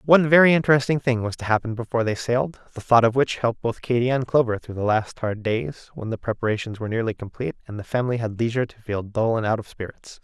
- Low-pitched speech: Yes, low, 120 Hz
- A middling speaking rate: No, fast, 245 wpm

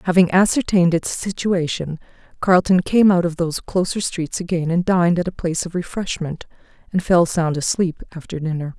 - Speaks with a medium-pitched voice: Yes, medium, 175 Hz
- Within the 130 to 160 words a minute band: No, average, 170 wpm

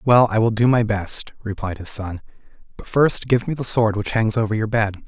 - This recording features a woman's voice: No, male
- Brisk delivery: Yes, fast, 235 wpm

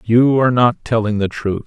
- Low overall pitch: Yes, low, 115 Hz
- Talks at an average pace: No, fast, 215 wpm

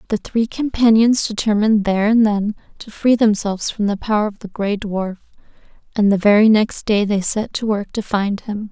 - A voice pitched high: Yes, high, 210 Hz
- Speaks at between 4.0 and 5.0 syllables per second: No, 5.2 syllables/s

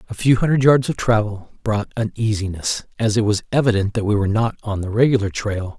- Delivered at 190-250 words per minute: Yes, fast, 205 wpm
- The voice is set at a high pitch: No, low, 110 Hz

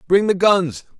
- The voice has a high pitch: No, medium, 180 Hz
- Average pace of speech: Yes, average, 180 wpm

